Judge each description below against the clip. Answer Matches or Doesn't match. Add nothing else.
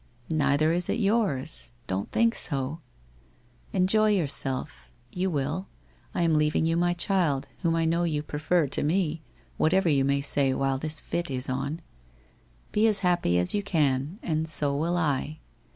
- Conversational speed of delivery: Matches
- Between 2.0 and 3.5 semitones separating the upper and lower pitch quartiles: Doesn't match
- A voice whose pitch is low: Doesn't match